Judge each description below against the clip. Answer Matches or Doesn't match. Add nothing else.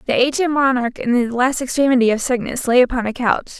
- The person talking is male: Doesn't match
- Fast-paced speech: Matches